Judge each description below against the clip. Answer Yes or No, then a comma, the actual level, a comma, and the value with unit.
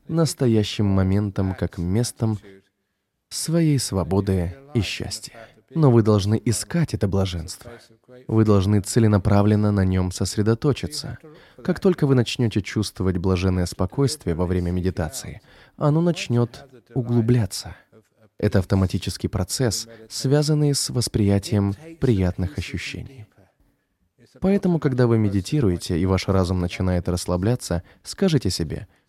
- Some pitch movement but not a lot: Yes, average, 4.6 semitones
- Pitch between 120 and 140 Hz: No, low, 105 Hz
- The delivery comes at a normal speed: No, slow, 105 wpm